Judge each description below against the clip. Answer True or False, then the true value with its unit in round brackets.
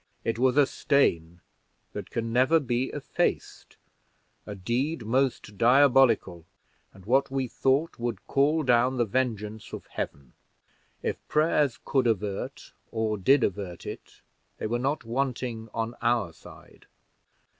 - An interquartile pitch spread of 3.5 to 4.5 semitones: True (3.8 semitones)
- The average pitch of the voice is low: True (120 Hz)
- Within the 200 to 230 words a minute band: False (135 wpm)